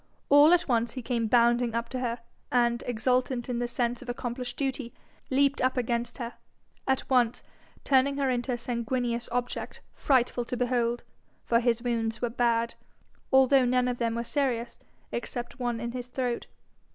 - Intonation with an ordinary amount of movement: No, narrow, 1.4 semitones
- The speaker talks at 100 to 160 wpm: No, average, 170 wpm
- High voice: Yes, high, 245 Hz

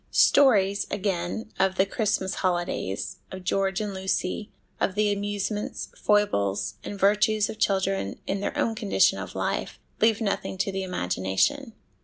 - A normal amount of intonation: No, narrow, 1.9 semitones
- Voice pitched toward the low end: No, high, 195 Hz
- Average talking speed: Yes, average, 145 wpm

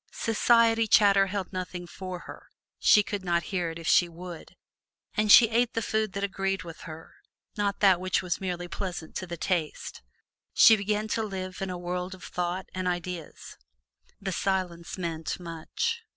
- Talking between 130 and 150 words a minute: No, average, 175 wpm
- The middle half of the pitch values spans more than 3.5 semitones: No, narrow, 2.5 semitones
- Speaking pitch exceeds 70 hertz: Yes, medium, 185 Hz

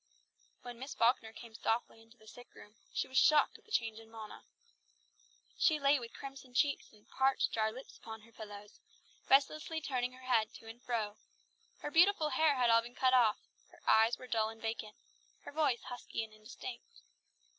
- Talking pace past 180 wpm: Yes, average, 190 wpm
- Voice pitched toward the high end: Yes, high, 240 Hz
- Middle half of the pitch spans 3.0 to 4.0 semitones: Yes, average, 3.3 semitones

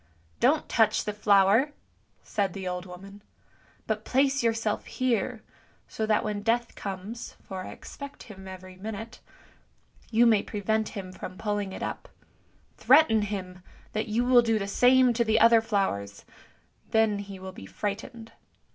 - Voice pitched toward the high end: Yes, high, 215 Hz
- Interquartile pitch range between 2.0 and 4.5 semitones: Yes, average, 2.9 semitones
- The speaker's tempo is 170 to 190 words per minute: No, average, 160 wpm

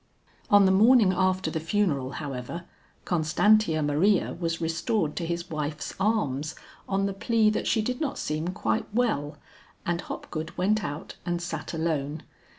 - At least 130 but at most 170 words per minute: Yes, average, 155 wpm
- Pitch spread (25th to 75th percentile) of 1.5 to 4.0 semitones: No, average, 4.8 semitones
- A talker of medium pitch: Yes, medium, 170 Hz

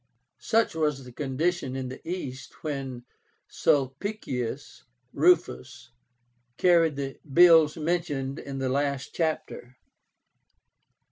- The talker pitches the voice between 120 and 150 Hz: Yes, medium, 140 Hz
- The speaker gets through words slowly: Yes, slow, 95 wpm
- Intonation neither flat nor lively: Yes, average, 3.9 semitones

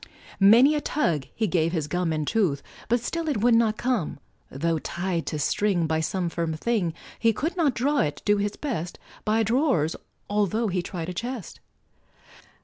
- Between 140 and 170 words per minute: No, average, 180 wpm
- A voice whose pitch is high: Yes, high, 200 Hz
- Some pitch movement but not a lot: No, wide, 6.1 semitones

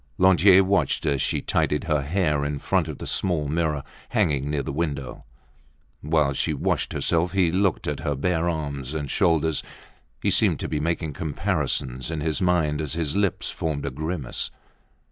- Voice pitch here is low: Yes, very low, 80 Hz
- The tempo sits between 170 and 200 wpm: Yes, average, 175 wpm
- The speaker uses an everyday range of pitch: Yes, average, 3.1 semitones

